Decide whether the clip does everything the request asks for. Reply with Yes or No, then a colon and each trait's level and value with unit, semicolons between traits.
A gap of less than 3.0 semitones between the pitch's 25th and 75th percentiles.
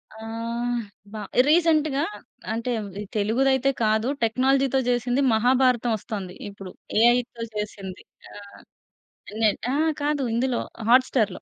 No: average, 3.3 semitones